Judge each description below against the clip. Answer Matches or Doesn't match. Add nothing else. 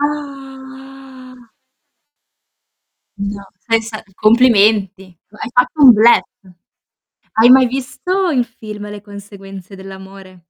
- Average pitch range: Matches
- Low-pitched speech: Doesn't match